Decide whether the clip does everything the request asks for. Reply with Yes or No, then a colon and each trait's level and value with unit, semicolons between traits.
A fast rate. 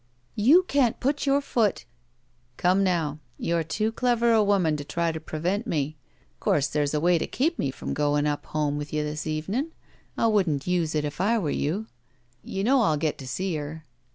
Yes: fast, 210 wpm